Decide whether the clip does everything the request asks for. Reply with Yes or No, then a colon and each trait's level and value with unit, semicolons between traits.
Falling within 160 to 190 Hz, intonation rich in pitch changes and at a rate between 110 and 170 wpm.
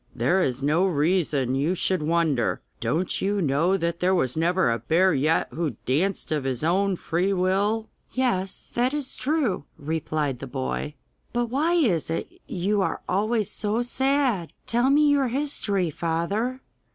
Yes: medium, 185 Hz; wide, 6.2 semitones; average, 160 wpm